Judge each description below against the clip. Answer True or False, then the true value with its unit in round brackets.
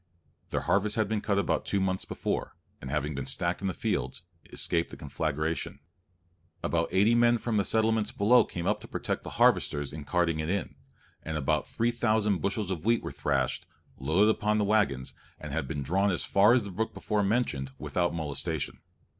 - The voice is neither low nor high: False (95 Hz)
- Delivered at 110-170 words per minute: False (195 wpm)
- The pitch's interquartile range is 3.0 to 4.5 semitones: False (5.6 semitones)